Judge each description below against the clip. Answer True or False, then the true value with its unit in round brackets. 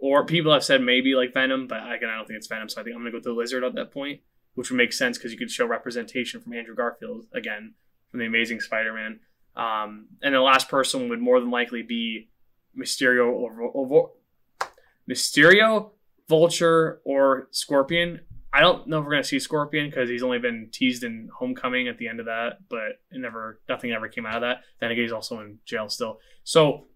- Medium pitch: False (130 Hz)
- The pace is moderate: False (220 wpm)